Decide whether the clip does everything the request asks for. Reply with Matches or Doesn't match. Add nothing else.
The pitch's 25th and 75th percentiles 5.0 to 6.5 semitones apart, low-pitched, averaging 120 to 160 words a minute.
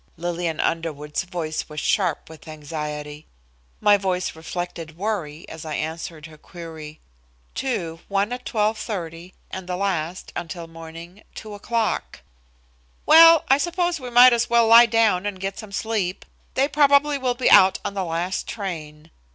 Doesn't match